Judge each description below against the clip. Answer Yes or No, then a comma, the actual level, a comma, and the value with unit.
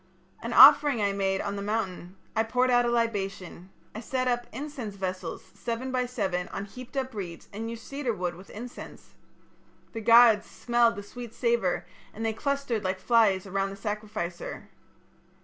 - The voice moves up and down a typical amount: Yes, average, 3.7 semitones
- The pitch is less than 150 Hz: No, high, 220 Hz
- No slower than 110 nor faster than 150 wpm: No, average, 170 wpm